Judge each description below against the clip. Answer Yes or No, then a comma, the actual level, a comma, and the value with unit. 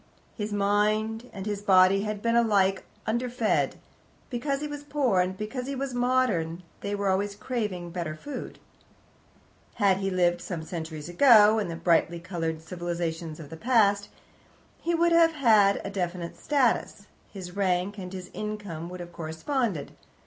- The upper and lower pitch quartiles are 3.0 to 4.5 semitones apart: No, average, 4.9 semitones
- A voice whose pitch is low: No, high, 200 Hz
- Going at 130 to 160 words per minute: Yes, average, 155 wpm